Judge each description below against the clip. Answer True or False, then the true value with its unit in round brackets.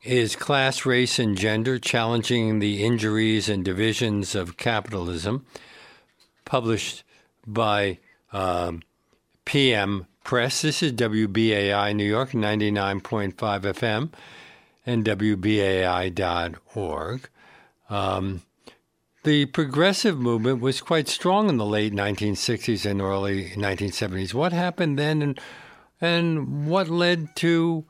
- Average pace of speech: False (105 wpm)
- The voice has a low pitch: True (110 Hz)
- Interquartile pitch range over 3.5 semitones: True (5.1 semitones)